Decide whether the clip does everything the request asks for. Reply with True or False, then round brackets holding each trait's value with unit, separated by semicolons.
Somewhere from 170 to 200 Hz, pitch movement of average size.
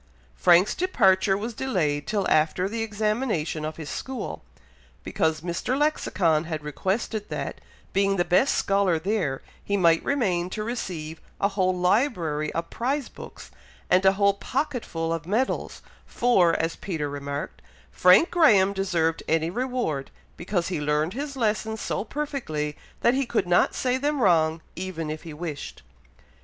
False (185 Hz; 5.7 semitones)